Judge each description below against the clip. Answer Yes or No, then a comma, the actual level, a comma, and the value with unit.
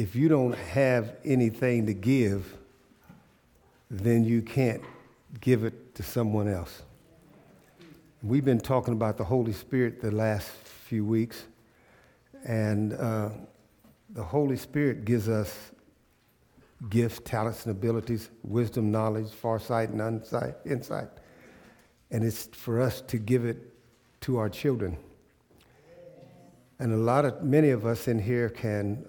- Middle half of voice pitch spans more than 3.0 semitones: No, average, 2.7 semitones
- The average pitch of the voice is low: Yes, low, 115 Hz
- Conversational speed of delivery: No, slow, 130 wpm